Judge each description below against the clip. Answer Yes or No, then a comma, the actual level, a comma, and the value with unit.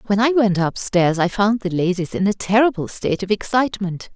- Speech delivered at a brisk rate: Yes, fast, 215 wpm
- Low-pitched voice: No, high, 200 Hz